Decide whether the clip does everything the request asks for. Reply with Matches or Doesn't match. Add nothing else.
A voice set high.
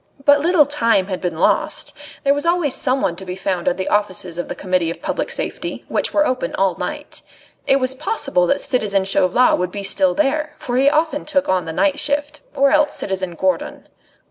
Matches